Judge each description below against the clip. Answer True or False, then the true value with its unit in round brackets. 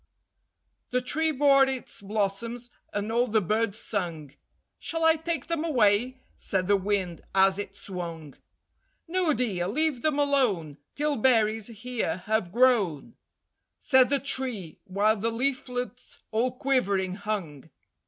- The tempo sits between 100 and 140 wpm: True (135 wpm)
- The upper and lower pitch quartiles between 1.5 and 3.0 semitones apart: False (5.0 semitones)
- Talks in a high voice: True (225 Hz)